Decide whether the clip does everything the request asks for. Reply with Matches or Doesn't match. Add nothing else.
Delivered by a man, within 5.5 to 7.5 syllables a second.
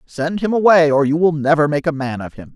Matches